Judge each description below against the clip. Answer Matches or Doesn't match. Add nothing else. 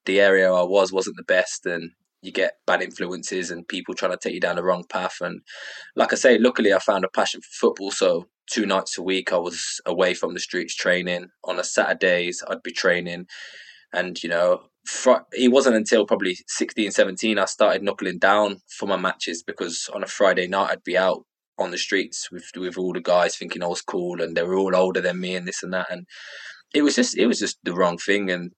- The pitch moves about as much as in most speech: Doesn't match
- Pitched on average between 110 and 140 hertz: Doesn't match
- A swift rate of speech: Matches